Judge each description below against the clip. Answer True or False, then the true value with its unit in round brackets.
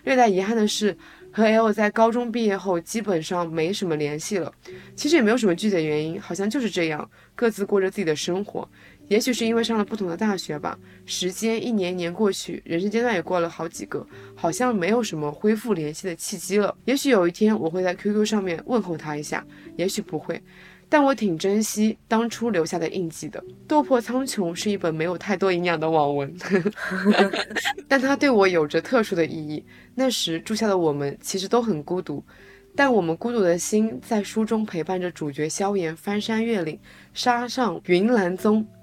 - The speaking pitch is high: True (195 Hz)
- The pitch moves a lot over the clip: False (4.8 semitones)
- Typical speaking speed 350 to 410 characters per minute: False (300 characters per minute)